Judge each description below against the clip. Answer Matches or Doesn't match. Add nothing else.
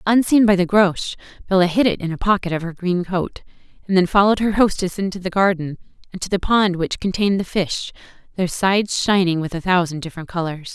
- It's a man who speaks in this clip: Doesn't match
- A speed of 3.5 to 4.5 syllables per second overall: Doesn't match